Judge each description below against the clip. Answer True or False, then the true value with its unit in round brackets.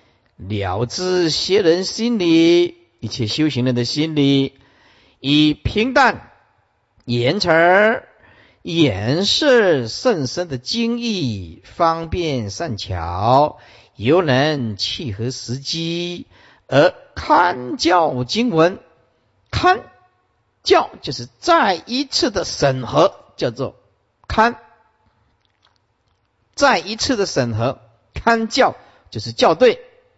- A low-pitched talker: False (150 Hz)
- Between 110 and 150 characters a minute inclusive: True (130 characters per minute)